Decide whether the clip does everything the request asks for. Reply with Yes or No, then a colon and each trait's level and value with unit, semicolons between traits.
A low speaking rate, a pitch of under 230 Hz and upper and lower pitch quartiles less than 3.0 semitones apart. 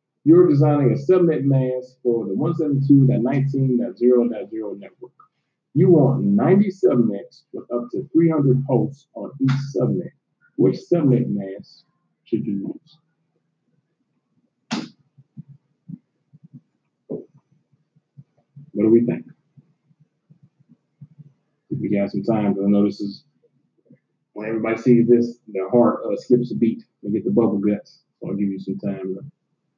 No: slow, 120 wpm; medium, 140 Hz; average, 4.8 semitones